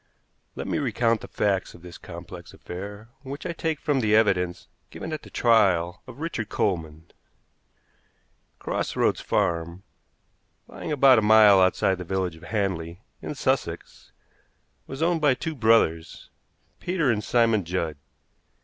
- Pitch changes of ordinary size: No, wide, 6.8 semitones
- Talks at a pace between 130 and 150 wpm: Yes, average, 145 wpm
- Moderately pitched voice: No, low, 105 Hz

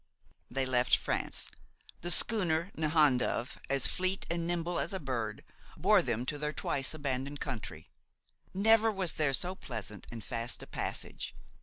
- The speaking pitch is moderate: Yes, medium, 145 Hz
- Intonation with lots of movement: Yes, wide, 5.9 semitones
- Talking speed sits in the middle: Yes, average, 150 wpm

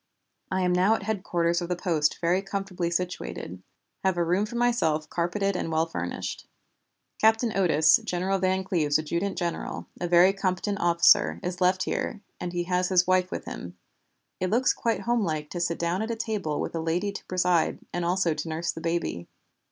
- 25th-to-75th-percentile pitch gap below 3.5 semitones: Yes, narrow, 2.5 semitones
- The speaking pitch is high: No, medium, 180 Hz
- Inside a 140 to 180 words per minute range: No, average, 190 wpm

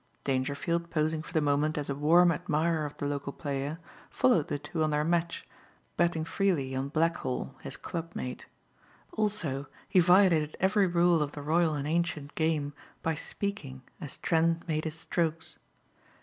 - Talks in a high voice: No, medium, 160 Hz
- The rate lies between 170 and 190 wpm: No, average, 160 wpm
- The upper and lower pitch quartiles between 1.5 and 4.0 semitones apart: Yes, average, 2.8 semitones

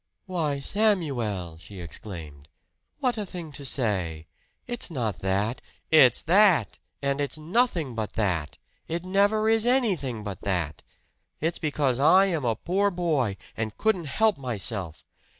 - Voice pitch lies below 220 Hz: Yes, medium, 140 Hz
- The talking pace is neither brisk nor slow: Yes, average, 145 wpm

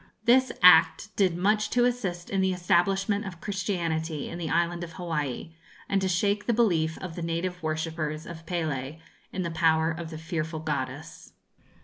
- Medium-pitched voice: Yes, medium, 170 Hz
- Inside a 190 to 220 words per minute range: No, average, 170 wpm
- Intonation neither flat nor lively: Yes, average, 3.1 semitones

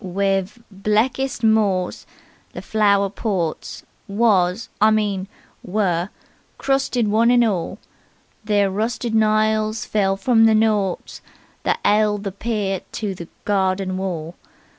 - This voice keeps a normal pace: No, slow, 120 wpm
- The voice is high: Yes, high, 205 Hz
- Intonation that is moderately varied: No, narrow, 2.2 semitones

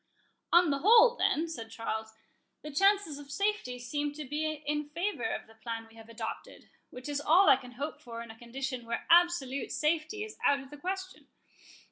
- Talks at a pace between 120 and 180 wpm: No, average, 195 wpm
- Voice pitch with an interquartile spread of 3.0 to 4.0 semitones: No, wide, 5.6 semitones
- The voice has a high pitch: Yes, very high, 290 Hz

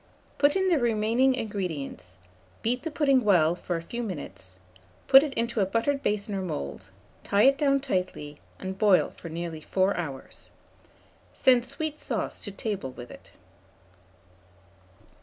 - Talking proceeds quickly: No, average, 150 wpm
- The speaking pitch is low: No, high, 205 Hz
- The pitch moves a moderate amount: No, wide, 7.4 semitones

